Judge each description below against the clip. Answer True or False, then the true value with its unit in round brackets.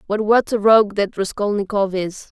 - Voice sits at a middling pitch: False (205 Hz)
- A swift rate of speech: False (175 wpm)